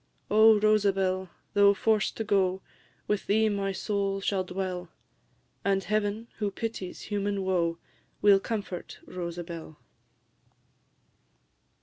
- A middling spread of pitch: No, narrow, 2.0 semitones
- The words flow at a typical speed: No, slow, 105 wpm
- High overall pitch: Yes, high, 195 Hz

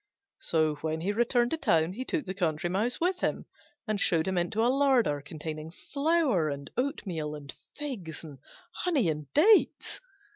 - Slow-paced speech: No, average, 170 wpm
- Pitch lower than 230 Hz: Yes, high, 190 Hz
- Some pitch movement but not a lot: No, wide, 8.9 semitones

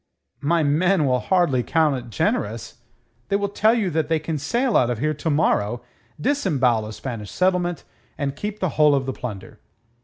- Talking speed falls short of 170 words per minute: No, average, 185 wpm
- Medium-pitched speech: Yes, medium, 150 Hz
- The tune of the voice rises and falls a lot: Yes, wide, 6.3 semitones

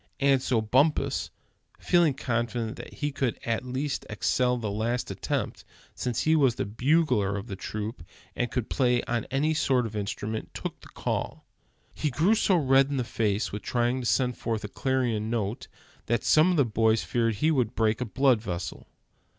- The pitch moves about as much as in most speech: Yes, average, 3.5 semitones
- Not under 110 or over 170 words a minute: No, average, 185 wpm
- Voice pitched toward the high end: No, low, 120 Hz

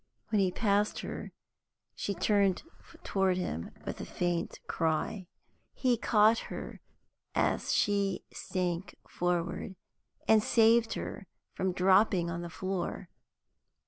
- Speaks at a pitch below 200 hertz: Yes, high, 190 Hz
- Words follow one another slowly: Yes, slow, 115 wpm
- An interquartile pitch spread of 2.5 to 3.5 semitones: Yes, average, 2.9 semitones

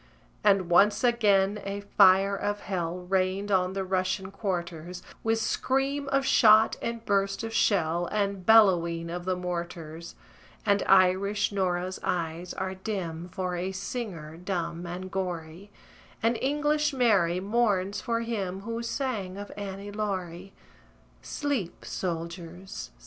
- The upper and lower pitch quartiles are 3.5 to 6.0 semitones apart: No, average, 2.9 semitones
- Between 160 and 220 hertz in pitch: Yes, high, 190 Hz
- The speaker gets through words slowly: Yes, slow, 130 wpm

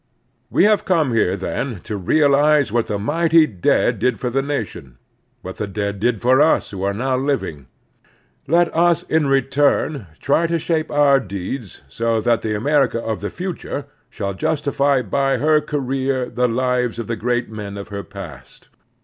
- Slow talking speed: No, average, 175 wpm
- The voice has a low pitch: Yes, low, 125 Hz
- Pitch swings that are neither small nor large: No, wide, 5.7 semitones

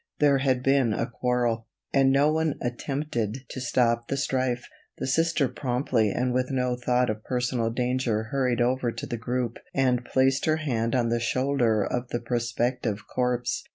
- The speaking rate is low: No, average, 170 wpm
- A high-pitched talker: No, low, 125 Hz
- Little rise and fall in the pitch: Yes, narrow, 2.1 semitones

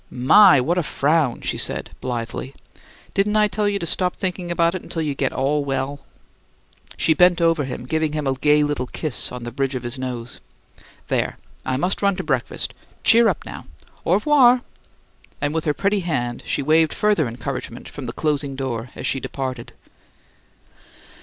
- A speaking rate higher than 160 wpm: Yes, average, 180 wpm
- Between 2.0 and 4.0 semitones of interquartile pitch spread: No, average, 5.3 semitones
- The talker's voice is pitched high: No, medium, 150 Hz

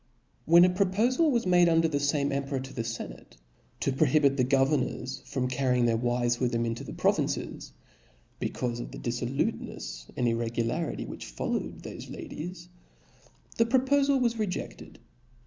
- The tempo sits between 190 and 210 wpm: No, average, 155 wpm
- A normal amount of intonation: No, wide, 6.6 semitones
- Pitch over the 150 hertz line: No, low, 135 Hz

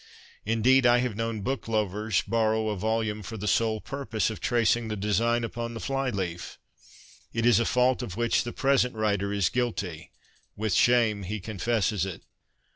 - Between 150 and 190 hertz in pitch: No, low, 110 Hz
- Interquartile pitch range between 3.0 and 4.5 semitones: No, narrow, 2.4 semitones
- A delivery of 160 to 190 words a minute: Yes, average, 175 wpm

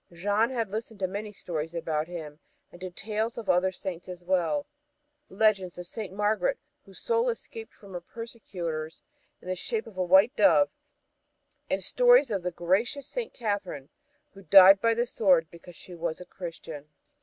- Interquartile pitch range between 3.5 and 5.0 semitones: Yes, average, 4.4 semitones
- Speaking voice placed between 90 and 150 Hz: No, high, 190 Hz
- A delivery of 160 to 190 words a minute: Yes, average, 175 wpm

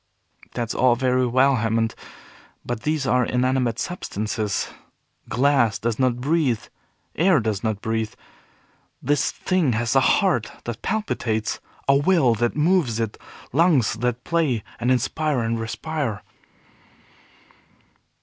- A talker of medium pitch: No, low, 125 Hz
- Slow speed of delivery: Yes, slow, 120 wpm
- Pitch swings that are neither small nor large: Yes, average, 4.1 semitones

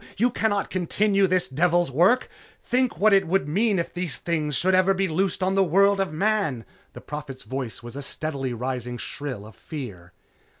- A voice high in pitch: No, medium, 170 Hz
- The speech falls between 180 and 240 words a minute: Yes, average, 185 wpm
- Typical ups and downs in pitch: No, wide, 6.4 semitones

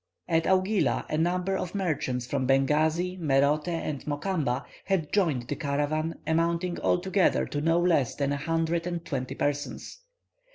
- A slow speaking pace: No, average, 150 wpm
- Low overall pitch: No, medium, 160 Hz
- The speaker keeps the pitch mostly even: No, average, 3.6 semitones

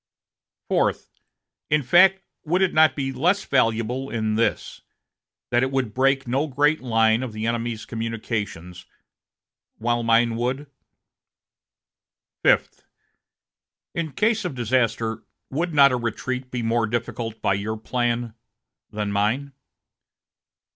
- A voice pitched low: Yes, low, 120 Hz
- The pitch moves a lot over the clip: No, average, 3.4 semitones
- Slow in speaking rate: Yes, slow, 120 wpm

